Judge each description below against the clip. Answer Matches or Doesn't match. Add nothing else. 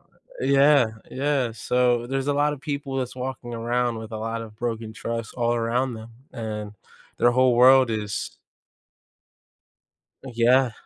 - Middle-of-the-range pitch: Doesn't match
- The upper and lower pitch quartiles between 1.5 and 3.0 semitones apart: Matches